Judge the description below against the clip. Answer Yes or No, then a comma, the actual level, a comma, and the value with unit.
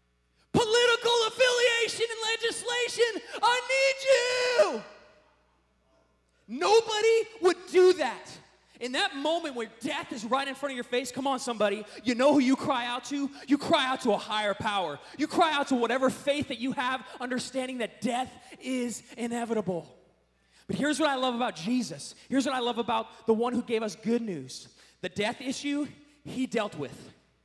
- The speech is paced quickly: No, average, 175 wpm